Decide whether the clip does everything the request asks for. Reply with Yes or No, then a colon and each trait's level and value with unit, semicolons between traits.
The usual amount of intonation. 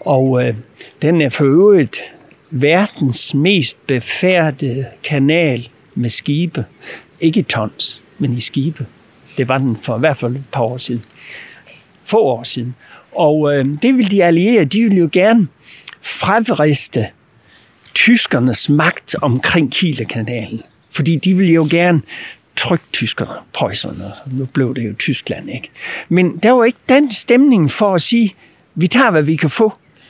No: wide, 6.0 semitones